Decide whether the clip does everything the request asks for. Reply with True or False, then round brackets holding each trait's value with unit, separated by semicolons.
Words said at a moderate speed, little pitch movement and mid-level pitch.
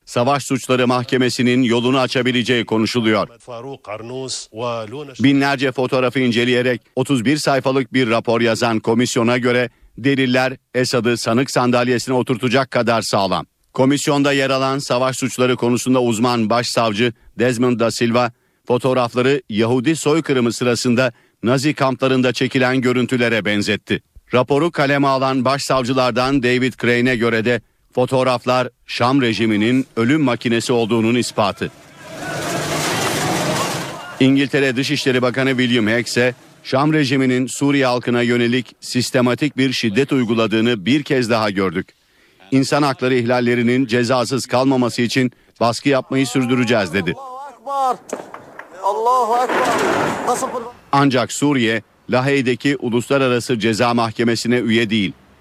False (105 wpm; 1.9 semitones; 125 Hz)